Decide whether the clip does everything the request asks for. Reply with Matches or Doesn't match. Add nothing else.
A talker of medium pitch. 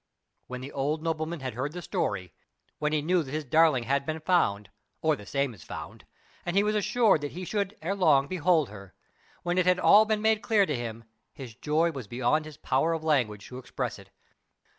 Matches